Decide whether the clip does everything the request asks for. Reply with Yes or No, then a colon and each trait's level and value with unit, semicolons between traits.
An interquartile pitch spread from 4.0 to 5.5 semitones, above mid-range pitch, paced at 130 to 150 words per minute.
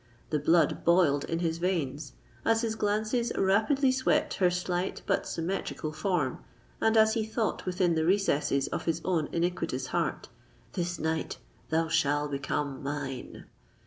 No: average, 5.1 semitones; medium, 170 Hz; average, 145 wpm